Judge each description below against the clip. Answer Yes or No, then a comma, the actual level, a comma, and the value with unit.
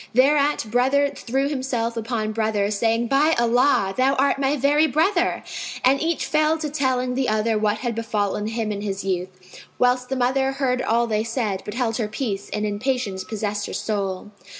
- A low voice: No, high, 235 Hz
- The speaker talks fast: No, average, 185 wpm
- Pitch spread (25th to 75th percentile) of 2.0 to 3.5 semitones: No, average, 4.2 semitones